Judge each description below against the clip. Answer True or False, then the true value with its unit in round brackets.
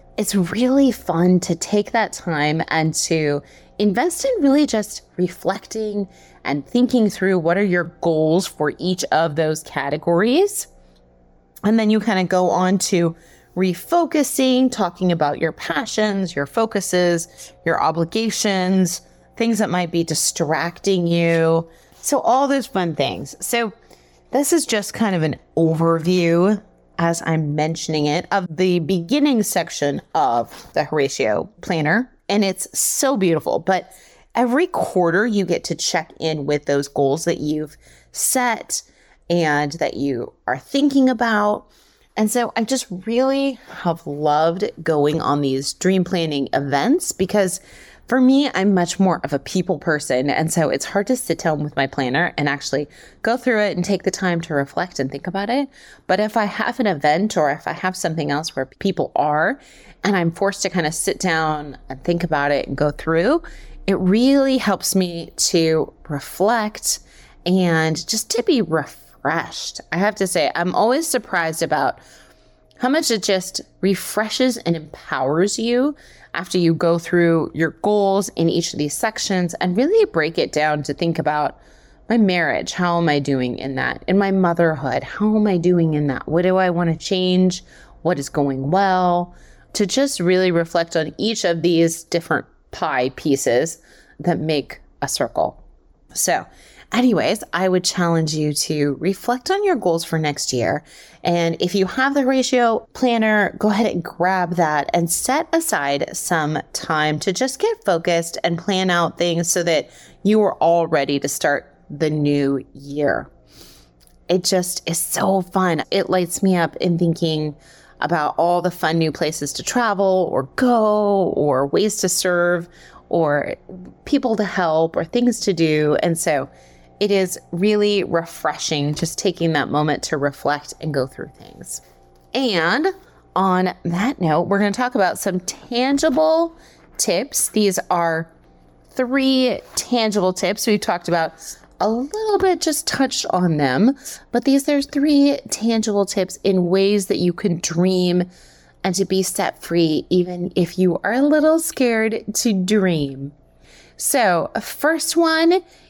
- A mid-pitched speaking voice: True (180 Hz)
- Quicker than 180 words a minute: False (160 wpm)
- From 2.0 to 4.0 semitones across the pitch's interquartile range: False (5.1 semitones)